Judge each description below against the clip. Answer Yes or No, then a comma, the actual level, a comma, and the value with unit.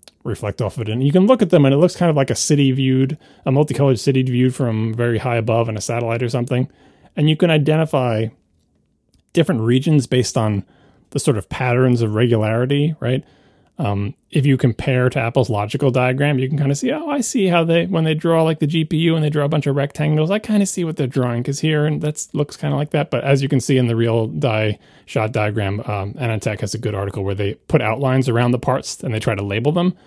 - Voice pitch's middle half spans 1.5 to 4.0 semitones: No, average, 4.7 semitones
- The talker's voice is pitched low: Yes, low, 130 Hz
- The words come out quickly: Yes, fast, 245 wpm